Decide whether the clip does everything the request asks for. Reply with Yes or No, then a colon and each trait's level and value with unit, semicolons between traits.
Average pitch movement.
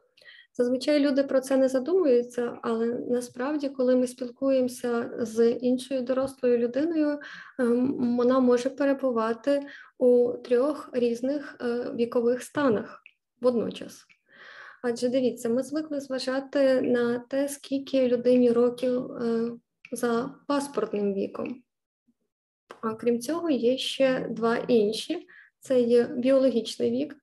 No: narrow, 2.2 semitones